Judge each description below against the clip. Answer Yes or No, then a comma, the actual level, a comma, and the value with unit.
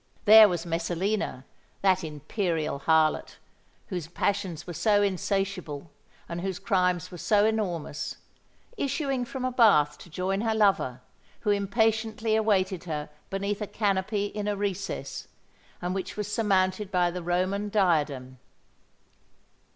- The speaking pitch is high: Yes, high, 195 Hz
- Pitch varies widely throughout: No, average, 3.4 semitones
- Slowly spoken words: Yes, slow, 125 wpm